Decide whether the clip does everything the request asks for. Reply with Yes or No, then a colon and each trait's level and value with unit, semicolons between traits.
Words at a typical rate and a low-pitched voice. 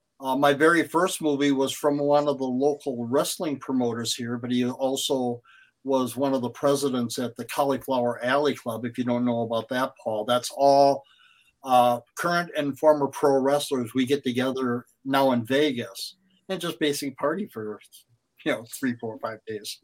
Yes: average, 180 wpm; low, 130 Hz